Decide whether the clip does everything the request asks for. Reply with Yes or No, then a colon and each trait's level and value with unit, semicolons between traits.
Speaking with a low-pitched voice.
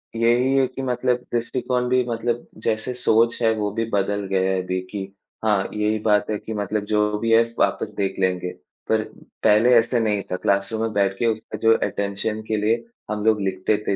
Yes: low, 110 Hz